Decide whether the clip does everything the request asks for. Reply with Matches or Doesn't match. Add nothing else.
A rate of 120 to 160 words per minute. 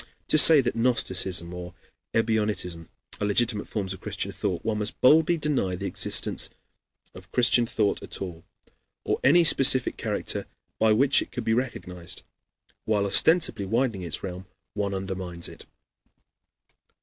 Matches